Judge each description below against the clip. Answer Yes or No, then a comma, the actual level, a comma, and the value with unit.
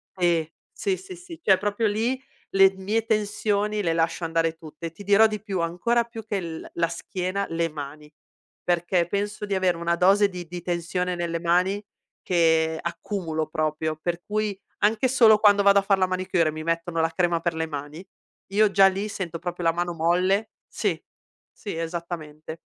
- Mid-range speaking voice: Yes, medium, 180 Hz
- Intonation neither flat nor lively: Yes, average, 3.5 semitones